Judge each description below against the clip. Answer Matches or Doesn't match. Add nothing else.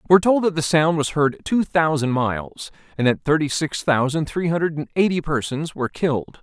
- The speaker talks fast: Doesn't match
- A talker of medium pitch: Matches